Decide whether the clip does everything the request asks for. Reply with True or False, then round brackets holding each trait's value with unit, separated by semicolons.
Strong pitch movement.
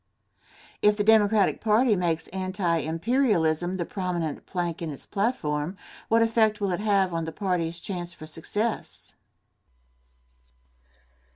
False (4.0 semitones)